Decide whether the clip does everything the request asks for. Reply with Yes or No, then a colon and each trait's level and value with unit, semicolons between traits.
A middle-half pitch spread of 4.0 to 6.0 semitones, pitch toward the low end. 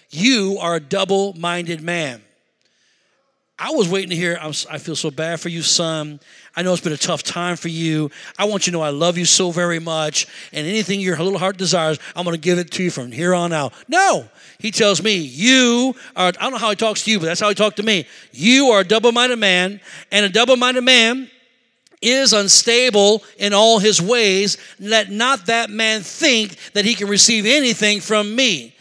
No: average, 4.7 semitones; high, 195 Hz